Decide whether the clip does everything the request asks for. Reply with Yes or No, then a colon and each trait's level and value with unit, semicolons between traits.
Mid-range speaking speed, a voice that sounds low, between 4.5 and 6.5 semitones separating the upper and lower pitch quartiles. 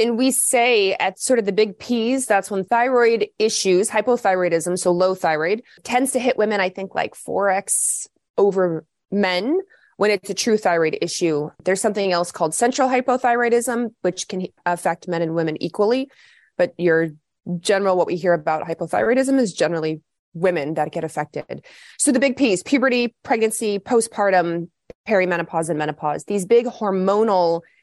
No: average, 155 wpm; high, 195 Hz; average, 5.3 semitones